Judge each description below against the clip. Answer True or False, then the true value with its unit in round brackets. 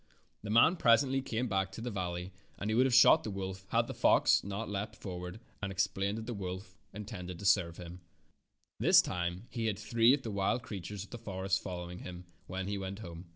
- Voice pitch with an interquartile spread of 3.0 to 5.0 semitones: True (3.5 semitones)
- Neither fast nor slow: False (215 wpm)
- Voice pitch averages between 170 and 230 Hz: False (100 Hz)